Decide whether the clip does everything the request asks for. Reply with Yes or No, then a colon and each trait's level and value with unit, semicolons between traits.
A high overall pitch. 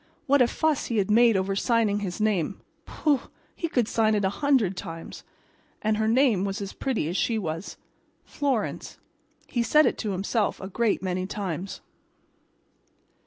Yes: high, 215 Hz